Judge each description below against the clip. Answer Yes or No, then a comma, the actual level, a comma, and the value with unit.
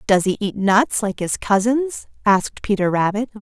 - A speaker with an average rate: Yes, average, 175 wpm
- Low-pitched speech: No, high, 210 Hz